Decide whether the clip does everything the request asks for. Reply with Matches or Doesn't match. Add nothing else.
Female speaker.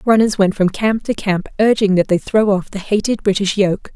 Matches